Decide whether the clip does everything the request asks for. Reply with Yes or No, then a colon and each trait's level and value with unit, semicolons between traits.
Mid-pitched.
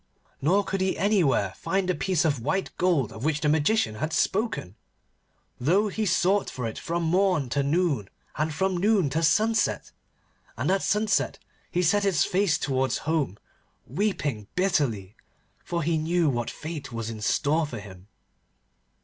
Yes: medium, 160 Hz